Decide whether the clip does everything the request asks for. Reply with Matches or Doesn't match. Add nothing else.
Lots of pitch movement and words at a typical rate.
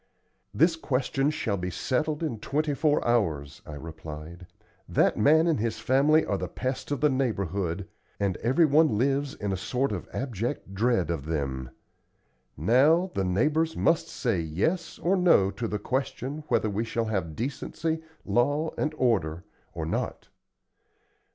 Matches